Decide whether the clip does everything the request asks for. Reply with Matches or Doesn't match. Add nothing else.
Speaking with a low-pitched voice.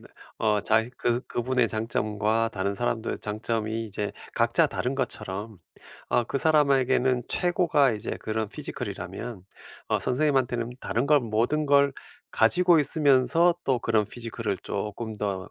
Matches